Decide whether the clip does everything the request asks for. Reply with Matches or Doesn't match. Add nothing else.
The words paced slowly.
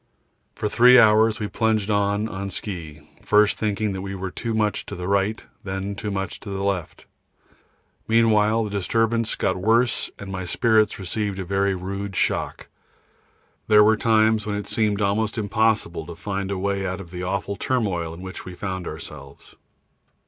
Doesn't match